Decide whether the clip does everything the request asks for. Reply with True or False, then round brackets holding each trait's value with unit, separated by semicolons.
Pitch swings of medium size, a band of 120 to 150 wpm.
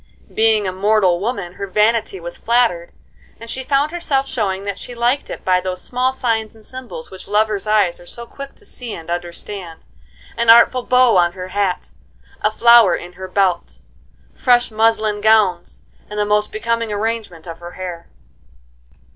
False (4.3 semitones; 170 wpm)